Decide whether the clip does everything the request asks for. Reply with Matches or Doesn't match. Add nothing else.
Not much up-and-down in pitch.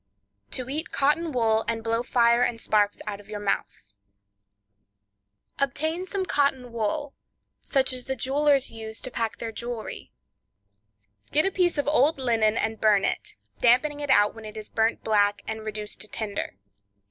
Doesn't match